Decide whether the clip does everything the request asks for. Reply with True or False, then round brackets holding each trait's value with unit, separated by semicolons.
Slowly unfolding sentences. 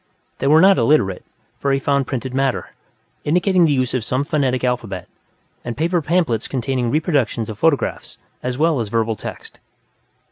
False (165 wpm)